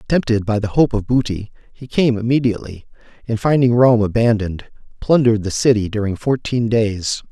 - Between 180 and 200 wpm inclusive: No, average, 155 wpm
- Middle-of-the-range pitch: No, low, 115 Hz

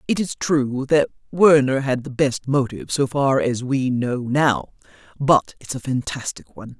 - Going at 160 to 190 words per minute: Yes, average, 175 wpm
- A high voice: No, low, 130 Hz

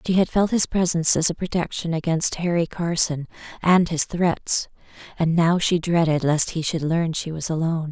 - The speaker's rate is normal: Yes, average, 190 wpm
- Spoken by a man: No, female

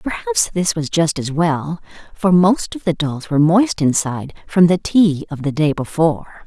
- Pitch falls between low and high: Yes, medium, 165 Hz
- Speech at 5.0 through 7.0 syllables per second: No, 4.6 syllables/s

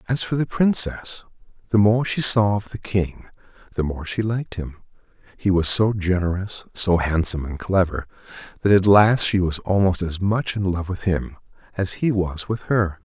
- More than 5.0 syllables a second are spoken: No, 4.8 syllables/s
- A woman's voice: No, male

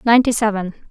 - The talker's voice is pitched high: Yes, high, 220 Hz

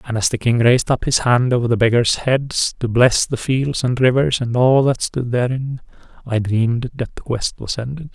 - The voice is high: No, low, 125 Hz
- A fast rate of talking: Yes, fast, 220 wpm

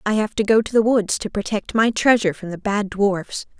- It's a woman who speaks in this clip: Yes, female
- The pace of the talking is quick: Yes, fast, 250 wpm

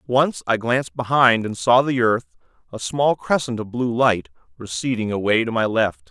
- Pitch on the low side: Yes, low, 115 Hz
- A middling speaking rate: Yes, average, 185 wpm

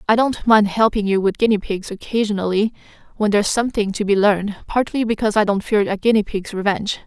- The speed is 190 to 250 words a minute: Yes, fast, 205 wpm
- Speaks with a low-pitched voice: No, high, 210 Hz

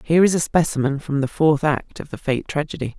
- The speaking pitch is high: No, medium, 145 Hz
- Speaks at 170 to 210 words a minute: No, fast, 240 wpm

